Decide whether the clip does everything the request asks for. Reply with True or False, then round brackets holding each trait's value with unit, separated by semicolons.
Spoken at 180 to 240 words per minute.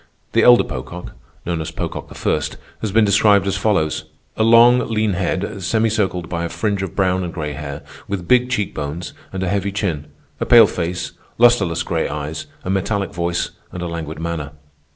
True (185 wpm)